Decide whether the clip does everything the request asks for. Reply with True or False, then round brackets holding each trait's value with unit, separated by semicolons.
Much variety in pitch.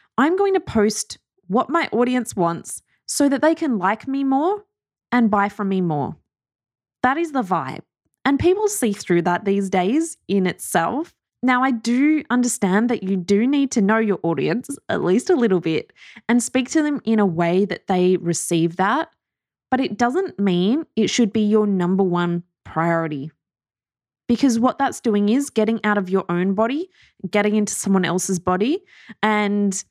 True (6.0 semitones)